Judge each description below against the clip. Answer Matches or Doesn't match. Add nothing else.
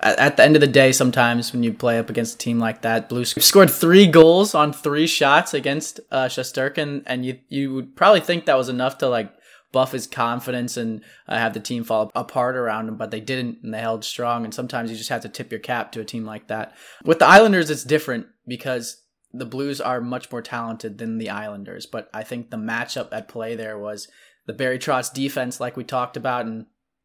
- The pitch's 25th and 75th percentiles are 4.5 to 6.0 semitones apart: Doesn't match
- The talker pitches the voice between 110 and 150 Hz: Matches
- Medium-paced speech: Doesn't match